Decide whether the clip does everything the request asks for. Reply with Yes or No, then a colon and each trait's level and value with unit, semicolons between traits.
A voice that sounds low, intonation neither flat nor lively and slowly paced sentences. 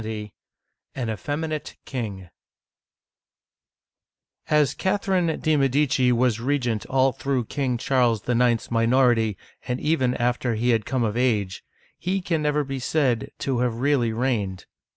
Yes: low, 125 Hz; average, 3.7 semitones; slow, 130 wpm